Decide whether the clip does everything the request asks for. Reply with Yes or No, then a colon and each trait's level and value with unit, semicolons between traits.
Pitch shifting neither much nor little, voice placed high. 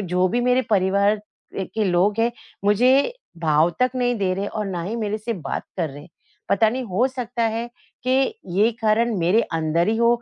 Yes: average, 4.2 semitones; high, 215 Hz